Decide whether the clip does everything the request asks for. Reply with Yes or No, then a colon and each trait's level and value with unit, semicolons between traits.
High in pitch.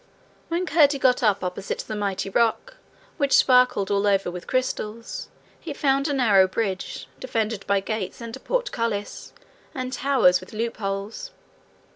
Yes: high, 225 Hz